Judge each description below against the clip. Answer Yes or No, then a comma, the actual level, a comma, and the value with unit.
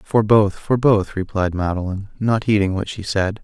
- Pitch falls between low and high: No, low, 100 Hz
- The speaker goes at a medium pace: Yes, average, 190 wpm